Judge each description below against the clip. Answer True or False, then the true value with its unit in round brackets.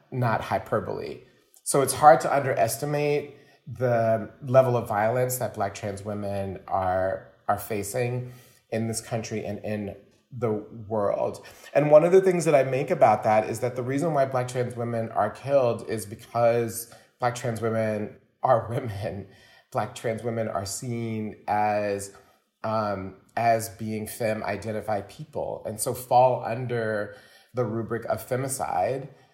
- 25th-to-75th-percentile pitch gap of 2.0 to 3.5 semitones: True (2.9 semitones)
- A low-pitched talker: True (115 Hz)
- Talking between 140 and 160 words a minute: True (145 wpm)